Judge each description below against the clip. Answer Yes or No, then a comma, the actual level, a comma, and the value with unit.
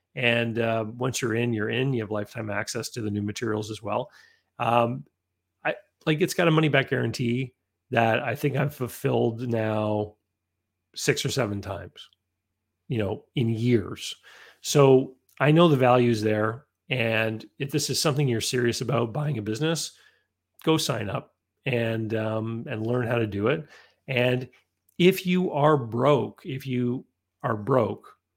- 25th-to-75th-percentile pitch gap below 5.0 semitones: Yes, average, 3.7 semitones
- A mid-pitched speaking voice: No, low, 120 Hz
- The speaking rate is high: No, average, 165 wpm